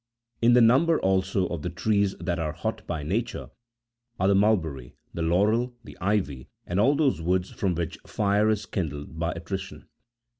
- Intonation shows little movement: No, average, 4.2 semitones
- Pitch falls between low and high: No, very low, 95 Hz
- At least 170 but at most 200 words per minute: Yes, average, 180 wpm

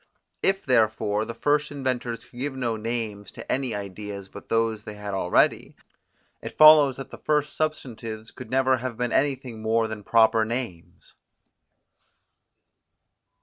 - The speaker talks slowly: No, average, 145 wpm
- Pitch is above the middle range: No, low, 115 Hz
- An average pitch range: Yes, average, 3.3 semitones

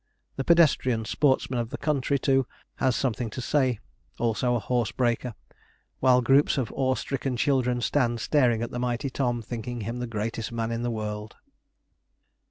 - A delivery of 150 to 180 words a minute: Yes, average, 170 wpm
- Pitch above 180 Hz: No, low, 125 Hz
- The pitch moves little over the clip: Yes, narrow, 2.3 semitones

